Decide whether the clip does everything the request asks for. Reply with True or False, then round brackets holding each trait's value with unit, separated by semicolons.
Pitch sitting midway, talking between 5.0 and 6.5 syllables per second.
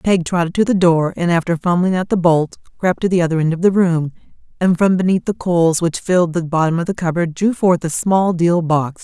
True (175 Hz; 5.5 syllables/s)